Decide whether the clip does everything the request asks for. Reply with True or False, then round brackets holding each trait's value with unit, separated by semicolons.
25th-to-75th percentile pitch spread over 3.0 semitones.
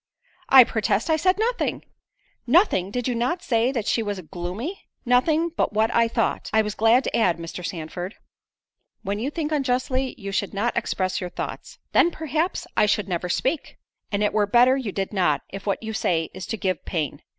True (5.3 semitones)